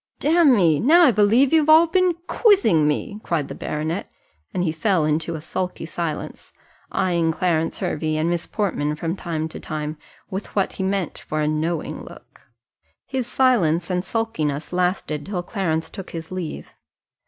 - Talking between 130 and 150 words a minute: No, average, 165 wpm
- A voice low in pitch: No, medium, 175 Hz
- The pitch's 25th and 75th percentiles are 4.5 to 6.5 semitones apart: Yes, average, 5.2 semitones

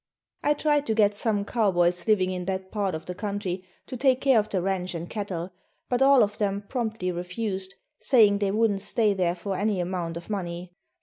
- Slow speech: No, average, 200 wpm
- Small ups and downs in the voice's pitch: No, average, 3.3 semitones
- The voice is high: Yes, high, 200 Hz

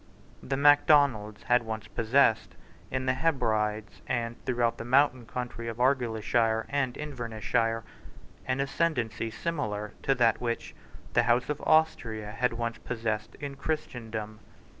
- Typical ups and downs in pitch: Yes, average, 3.3 semitones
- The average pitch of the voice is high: No, low, 120 Hz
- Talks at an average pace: No, slow, 130 wpm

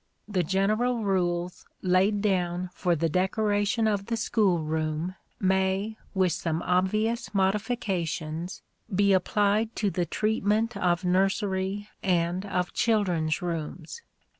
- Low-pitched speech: No, high, 190 Hz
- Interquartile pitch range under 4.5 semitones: Yes, average, 2.9 semitones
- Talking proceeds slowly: Yes, slow, 115 wpm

